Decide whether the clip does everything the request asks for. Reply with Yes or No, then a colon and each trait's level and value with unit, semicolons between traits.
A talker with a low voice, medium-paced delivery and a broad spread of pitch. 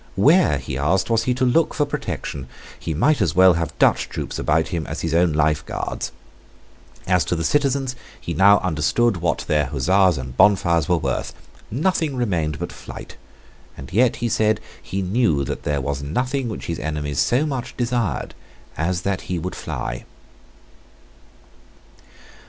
Yes: very low, 90 Hz; average, 165 wpm; wide, 7.8 semitones